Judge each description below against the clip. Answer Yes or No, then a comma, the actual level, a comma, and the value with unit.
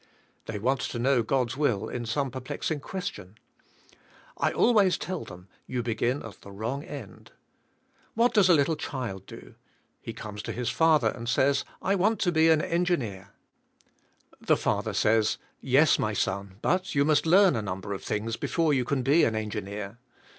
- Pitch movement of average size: No, wide, 6.8 semitones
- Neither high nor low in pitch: No, low, 125 Hz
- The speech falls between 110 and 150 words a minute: No, average, 185 wpm